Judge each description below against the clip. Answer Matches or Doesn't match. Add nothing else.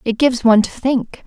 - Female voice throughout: Matches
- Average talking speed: Doesn't match